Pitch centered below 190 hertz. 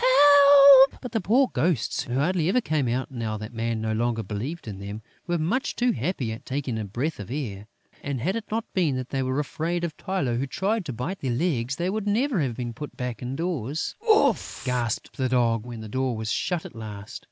Yes: low, 135 Hz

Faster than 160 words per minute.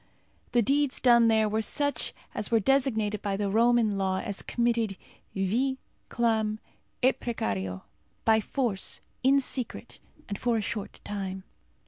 No: average, 140 wpm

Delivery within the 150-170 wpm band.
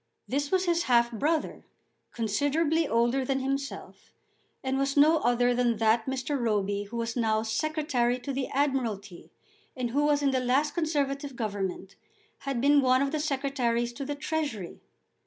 Yes: average, 155 wpm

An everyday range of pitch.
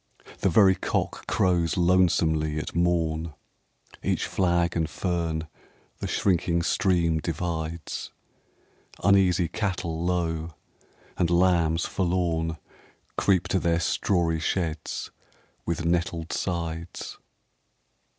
No: narrow, 1.7 semitones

